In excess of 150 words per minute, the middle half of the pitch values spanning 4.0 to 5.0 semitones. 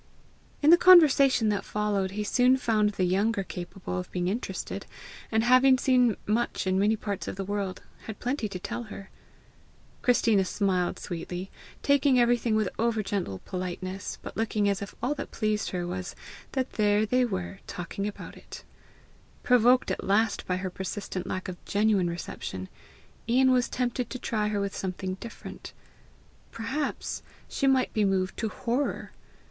Yes: average, 165 wpm; average, 4.3 semitones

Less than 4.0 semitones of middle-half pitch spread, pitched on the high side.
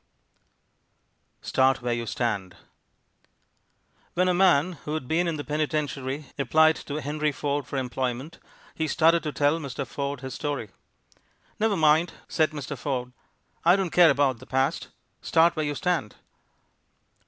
No: average, 3.2 semitones; medium, 145 Hz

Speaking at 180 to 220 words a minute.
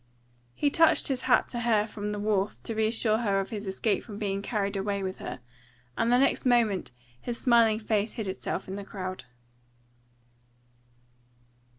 No: average, 170 wpm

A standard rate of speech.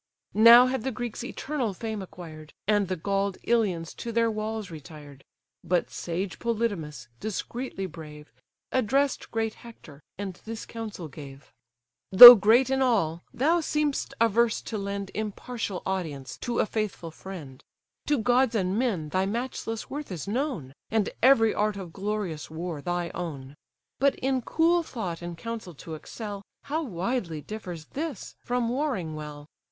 Yes: average, 150 wpm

